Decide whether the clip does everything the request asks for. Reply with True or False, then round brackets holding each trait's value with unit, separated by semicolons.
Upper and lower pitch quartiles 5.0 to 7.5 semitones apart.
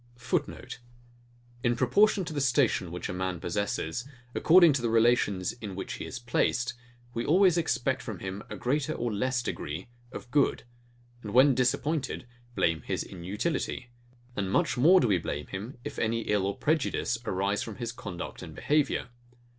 True (5.4 semitones)